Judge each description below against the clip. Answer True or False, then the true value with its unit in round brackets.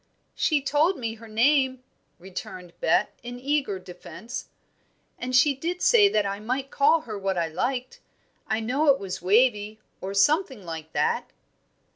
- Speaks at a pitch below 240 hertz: False (245 Hz)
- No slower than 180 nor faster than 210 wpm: False (155 wpm)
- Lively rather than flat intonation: True (6.0 semitones)